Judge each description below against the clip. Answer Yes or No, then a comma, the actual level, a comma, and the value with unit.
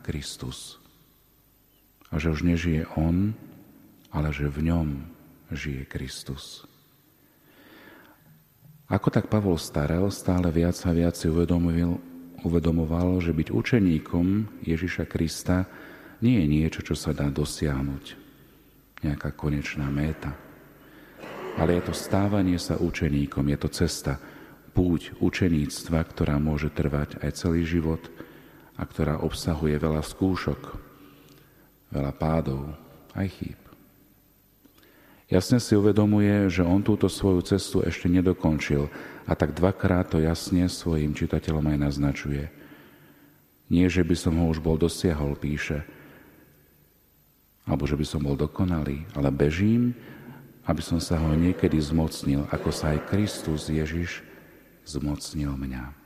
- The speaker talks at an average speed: Yes, average, 120 wpm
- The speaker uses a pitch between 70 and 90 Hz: Yes, very low, 80 Hz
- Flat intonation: No, average, 3.3 semitones